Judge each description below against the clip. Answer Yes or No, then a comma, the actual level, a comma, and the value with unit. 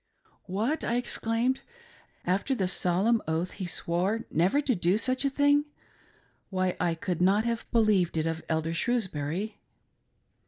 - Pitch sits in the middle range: No, high, 195 Hz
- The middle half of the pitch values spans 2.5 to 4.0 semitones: No, average, 5.3 semitones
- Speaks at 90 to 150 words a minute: Yes, average, 145 wpm